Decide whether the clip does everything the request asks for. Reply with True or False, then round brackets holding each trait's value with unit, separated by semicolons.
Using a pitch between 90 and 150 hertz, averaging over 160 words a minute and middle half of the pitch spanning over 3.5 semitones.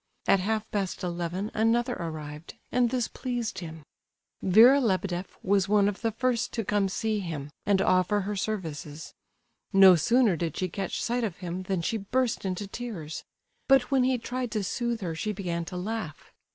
False (200 Hz; 180 wpm; 4.3 semitones)